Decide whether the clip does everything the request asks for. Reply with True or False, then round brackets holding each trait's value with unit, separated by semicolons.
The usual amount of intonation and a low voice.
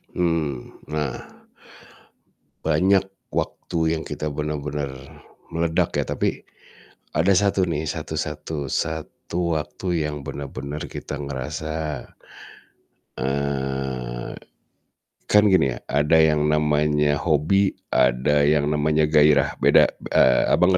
False (2.1 semitones; 75 Hz)